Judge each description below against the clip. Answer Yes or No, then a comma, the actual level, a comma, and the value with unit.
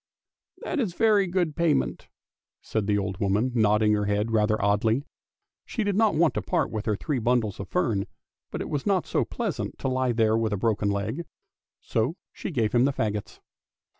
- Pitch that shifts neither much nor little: No, wide, 7.1 semitones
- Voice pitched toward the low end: Yes, low, 115 Hz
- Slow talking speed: No, average, 195 wpm